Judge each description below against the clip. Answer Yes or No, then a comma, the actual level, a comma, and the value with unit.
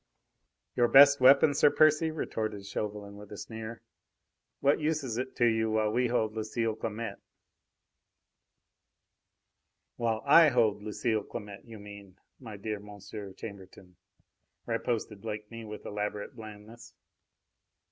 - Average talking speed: No, slow, 125 wpm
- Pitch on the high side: No, low, 110 Hz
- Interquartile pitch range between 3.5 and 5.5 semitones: No, narrow, 2.5 semitones